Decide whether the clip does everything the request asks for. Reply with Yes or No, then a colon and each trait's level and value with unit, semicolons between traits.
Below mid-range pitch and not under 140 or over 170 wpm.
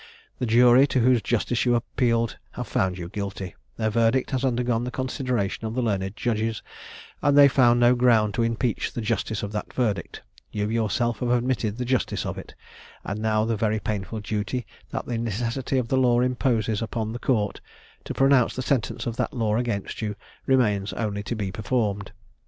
No: low, 115 Hz; average, 190 wpm